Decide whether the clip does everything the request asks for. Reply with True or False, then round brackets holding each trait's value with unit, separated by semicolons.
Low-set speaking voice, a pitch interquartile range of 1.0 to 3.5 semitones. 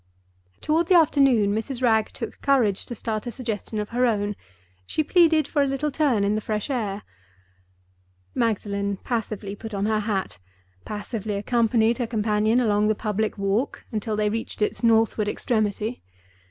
False (220 Hz; 2.8 semitones)